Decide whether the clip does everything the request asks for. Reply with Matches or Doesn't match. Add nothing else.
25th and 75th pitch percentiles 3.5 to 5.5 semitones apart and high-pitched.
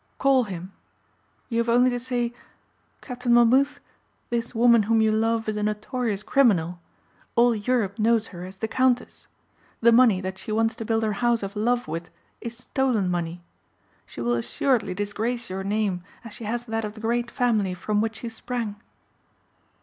Doesn't match